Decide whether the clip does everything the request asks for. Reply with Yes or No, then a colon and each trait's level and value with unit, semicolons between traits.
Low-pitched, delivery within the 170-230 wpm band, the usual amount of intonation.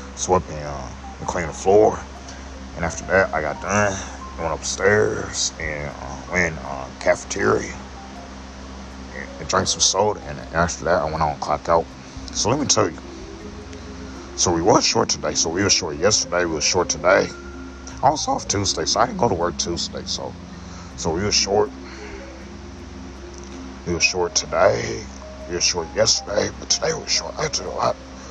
Yes: very low, 70 Hz; average, 190 wpm; average, 4.5 semitones